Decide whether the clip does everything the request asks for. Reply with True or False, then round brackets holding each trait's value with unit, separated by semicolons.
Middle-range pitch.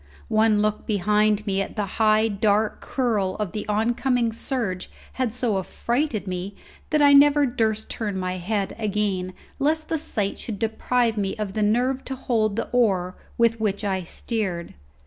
False (215 Hz)